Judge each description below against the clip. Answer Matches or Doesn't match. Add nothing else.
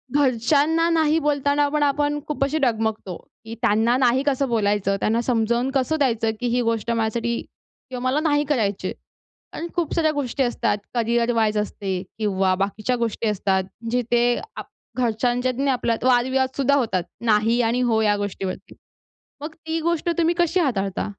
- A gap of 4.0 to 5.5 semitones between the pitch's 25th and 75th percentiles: Matches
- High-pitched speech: Matches